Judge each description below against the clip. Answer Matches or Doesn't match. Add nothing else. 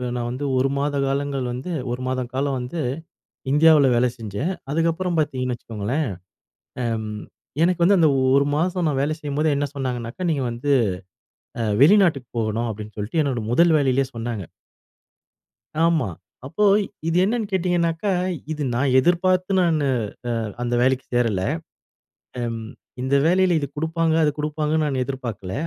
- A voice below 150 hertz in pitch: Matches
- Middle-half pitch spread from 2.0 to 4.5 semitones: Doesn't match